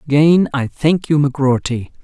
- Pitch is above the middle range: No, medium, 145 Hz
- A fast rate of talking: No, average, 145 wpm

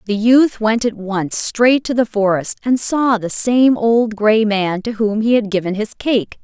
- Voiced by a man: No, female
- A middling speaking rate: No, fast, 215 wpm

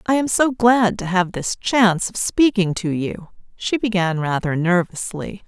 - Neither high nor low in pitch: No, high, 195 Hz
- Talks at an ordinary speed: Yes, average, 175 wpm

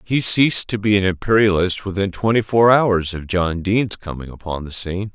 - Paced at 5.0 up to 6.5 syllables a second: Yes, 5.4 syllables/s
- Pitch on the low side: Yes, low, 100 Hz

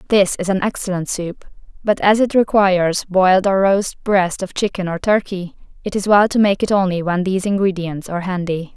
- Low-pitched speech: No, high, 190 Hz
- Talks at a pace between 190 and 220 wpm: Yes, average, 200 wpm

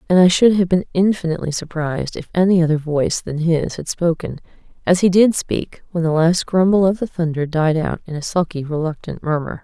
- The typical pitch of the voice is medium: Yes, medium, 170 Hz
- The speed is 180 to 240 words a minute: Yes, average, 200 wpm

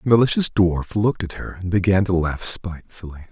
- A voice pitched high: No, very low, 95 Hz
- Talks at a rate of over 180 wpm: Yes, average, 200 wpm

